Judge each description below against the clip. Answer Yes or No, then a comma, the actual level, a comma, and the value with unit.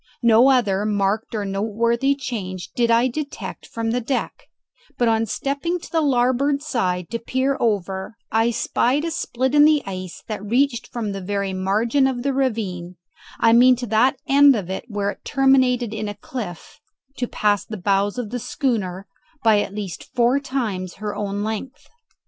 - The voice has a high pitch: Yes, high, 230 Hz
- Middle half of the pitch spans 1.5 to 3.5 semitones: No, average, 4.3 semitones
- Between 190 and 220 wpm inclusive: No, average, 180 wpm